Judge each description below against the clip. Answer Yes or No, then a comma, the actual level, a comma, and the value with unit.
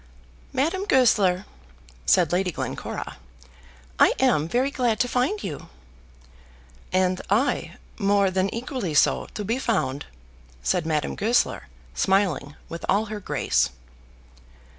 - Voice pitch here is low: No, high, 200 Hz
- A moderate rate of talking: No, slow, 120 wpm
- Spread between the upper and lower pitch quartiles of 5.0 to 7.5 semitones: Yes, wide, 5.5 semitones